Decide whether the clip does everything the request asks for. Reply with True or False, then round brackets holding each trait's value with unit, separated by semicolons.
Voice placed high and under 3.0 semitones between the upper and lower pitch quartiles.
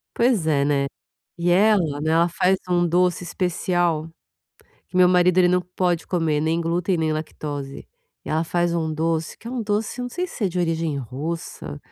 False (170 Hz; 2.5 semitones)